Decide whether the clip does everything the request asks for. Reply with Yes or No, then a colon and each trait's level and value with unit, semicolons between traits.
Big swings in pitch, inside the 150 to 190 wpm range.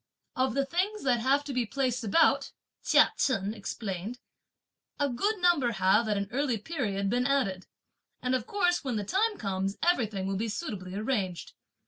Yes: wide, 5.9 semitones; average, 170 wpm